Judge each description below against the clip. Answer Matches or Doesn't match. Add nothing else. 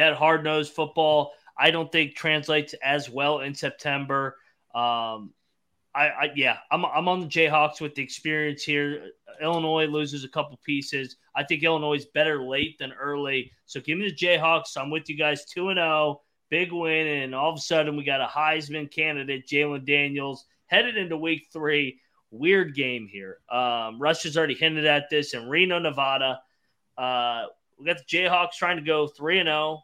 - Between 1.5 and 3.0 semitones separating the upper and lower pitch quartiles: Matches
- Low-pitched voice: Doesn't match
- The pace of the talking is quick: Doesn't match